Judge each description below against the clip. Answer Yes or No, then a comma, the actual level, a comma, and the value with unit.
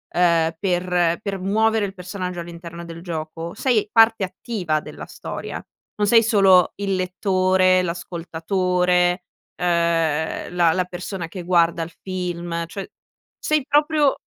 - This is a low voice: No, medium, 180 Hz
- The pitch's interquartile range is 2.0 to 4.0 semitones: Yes, narrow, 2.5 semitones